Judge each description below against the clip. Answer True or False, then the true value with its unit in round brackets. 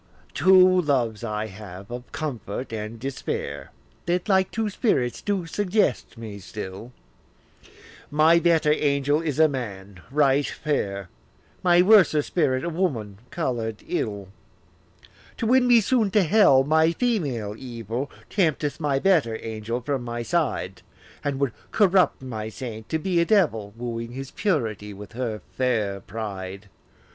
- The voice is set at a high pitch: False (135 Hz)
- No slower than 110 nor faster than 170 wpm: True (140 wpm)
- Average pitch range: False (7.4 semitones)